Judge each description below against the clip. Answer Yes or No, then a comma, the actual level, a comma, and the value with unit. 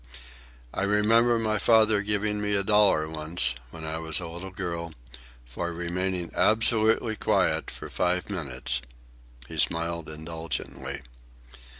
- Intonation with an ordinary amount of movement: Yes, average, 4.3 semitones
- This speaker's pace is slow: Yes, slow, 125 wpm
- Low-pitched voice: Yes, very low, 90 Hz